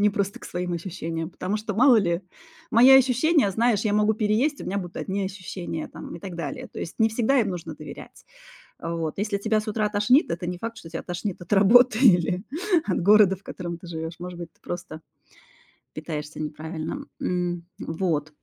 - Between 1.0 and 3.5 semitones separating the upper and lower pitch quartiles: No, average, 4.1 semitones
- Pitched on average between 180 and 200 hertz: Yes, high, 190 Hz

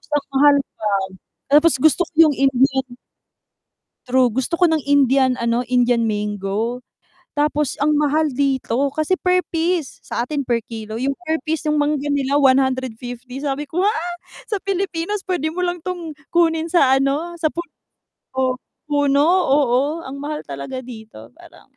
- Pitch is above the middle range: Yes, very high, 280 Hz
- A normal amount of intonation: Yes, average, 3.9 semitones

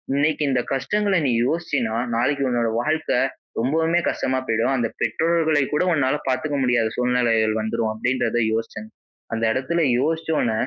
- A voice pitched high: No, low, 130 Hz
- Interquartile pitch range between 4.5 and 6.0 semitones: Yes, average, 5.1 semitones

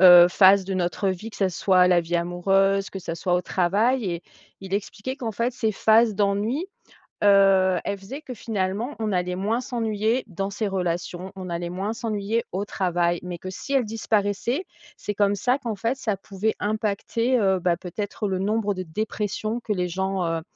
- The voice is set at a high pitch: Yes, high, 200 Hz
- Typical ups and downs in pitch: Yes, average, 3.1 semitones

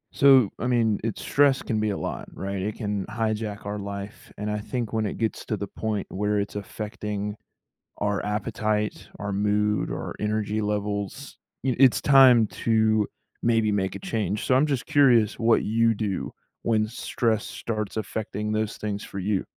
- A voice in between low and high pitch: No, low, 105 Hz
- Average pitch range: No, narrow, 1.7 semitones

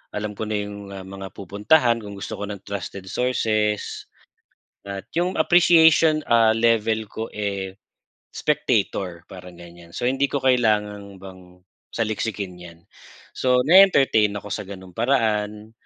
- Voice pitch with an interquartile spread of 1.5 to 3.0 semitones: No, average, 3.8 semitones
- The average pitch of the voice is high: No, low, 105 Hz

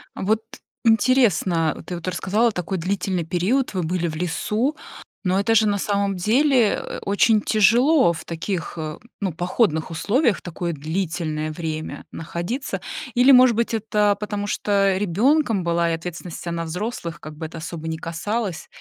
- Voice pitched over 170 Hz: Yes, high, 190 Hz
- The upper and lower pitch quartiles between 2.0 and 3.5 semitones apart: No, average, 4.7 semitones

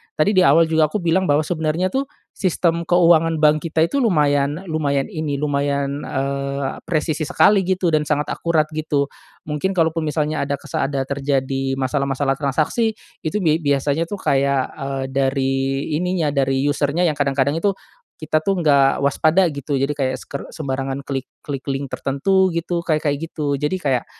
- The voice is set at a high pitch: No, medium, 150 Hz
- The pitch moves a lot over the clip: No, average, 2.8 semitones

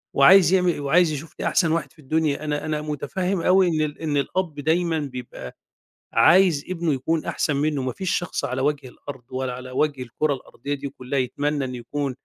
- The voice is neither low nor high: Yes, medium, 145 Hz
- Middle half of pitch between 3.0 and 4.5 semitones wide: Yes, average, 3.3 semitones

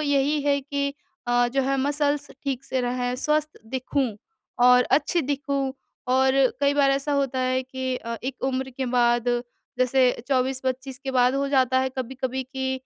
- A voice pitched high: Yes, very high, 265 Hz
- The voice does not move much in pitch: Yes, narrow, 1.6 semitones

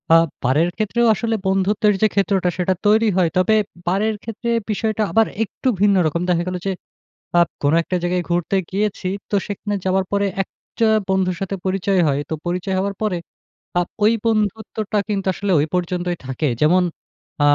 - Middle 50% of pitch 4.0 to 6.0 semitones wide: No, average, 2.8 semitones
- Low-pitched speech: No, high, 195 Hz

